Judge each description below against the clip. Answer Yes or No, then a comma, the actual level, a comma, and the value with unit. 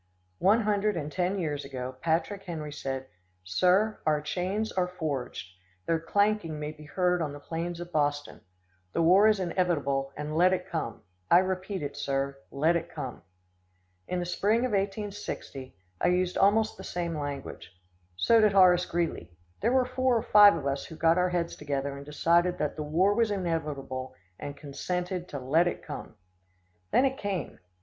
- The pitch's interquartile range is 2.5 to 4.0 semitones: No, average, 4.8 semitones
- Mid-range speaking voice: Yes, medium, 170 Hz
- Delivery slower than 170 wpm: No, average, 175 wpm